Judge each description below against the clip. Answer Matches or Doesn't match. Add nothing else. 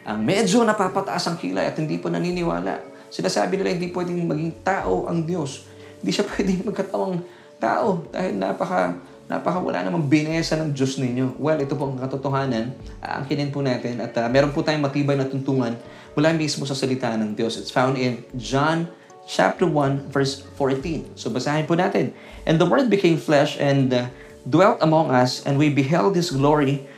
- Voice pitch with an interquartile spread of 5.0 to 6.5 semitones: Doesn't match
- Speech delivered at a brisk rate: Matches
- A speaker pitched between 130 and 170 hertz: Matches